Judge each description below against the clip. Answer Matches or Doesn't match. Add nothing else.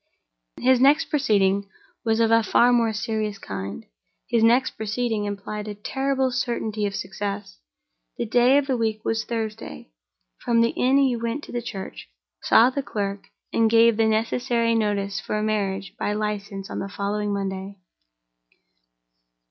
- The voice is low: Doesn't match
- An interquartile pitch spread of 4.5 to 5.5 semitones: Doesn't match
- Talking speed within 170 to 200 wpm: Doesn't match